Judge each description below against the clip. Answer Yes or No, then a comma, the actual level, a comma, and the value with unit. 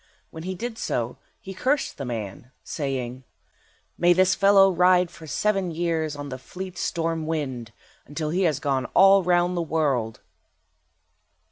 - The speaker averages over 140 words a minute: Yes, average, 150 wpm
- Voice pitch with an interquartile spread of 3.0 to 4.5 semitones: No, average, 5.0 semitones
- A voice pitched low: No, medium, 165 Hz